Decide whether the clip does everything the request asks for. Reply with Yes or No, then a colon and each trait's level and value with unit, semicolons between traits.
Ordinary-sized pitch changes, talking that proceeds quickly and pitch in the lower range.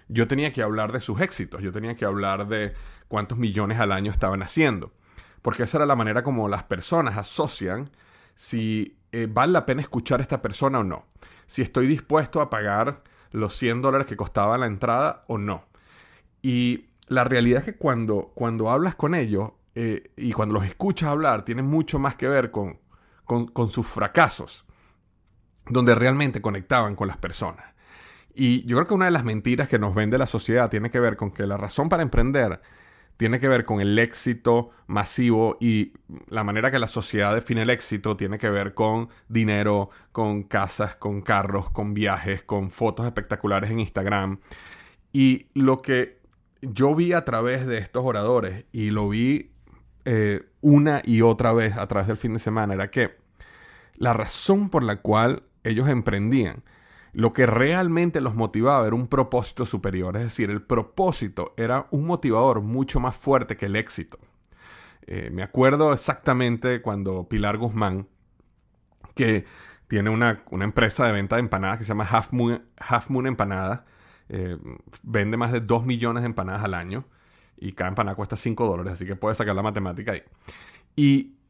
No: average, 3.8 semitones; average, 175 wpm; low, 115 Hz